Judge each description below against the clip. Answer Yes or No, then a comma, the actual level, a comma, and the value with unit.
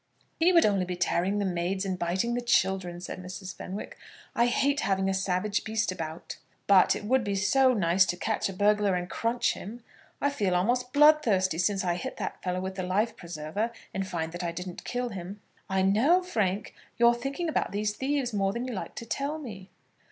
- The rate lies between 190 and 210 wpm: Yes, fast, 205 wpm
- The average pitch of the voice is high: Yes, high, 200 Hz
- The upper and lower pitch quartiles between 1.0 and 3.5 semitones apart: No, average, 4.5 semitones